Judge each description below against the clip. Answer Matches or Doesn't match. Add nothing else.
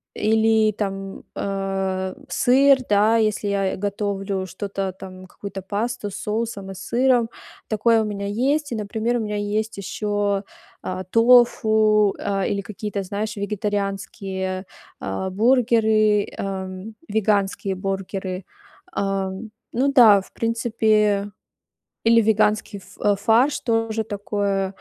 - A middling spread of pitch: Doesn't match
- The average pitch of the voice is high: Matches